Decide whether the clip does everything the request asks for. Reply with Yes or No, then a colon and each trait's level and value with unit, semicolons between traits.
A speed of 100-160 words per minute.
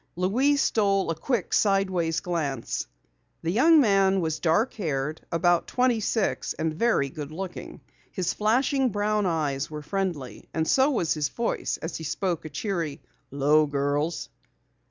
Yes: average, 150 wpm